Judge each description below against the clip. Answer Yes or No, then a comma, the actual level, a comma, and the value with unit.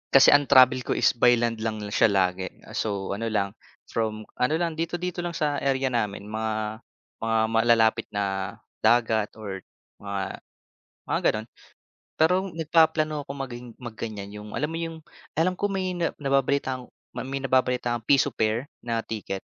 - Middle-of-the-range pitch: No, low, 120 Hz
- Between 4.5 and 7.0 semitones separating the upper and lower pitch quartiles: Yes, average, 5.0 semitones